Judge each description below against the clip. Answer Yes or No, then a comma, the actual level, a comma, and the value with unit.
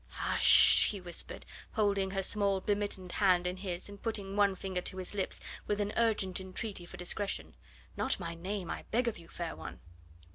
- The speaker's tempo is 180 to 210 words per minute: Yes, average, 195 wpm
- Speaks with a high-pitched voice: Yes, high, 195 Hz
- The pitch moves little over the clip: Yes, narrow, 2.2 semitones